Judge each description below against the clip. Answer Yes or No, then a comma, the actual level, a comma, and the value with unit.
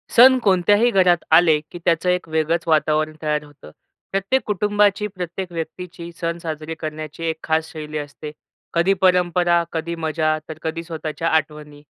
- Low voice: No, medium, 165 Hz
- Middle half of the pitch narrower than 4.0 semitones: Yes, narrow, 2.6 semitones